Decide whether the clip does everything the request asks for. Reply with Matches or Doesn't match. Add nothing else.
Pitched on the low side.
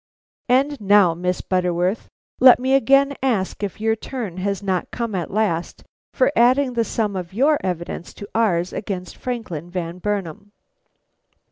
Doesn't match